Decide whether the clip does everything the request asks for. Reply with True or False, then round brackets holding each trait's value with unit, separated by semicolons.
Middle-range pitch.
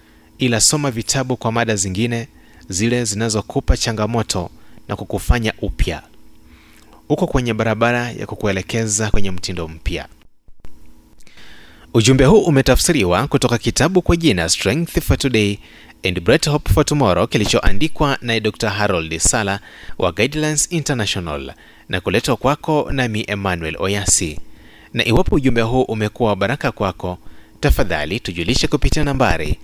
False (110 Hz)